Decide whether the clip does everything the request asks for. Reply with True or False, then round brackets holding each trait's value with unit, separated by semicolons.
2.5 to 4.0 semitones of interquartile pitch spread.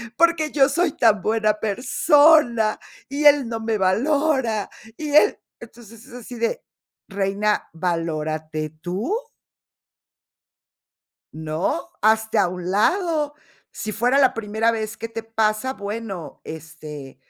False (5.6 semitones)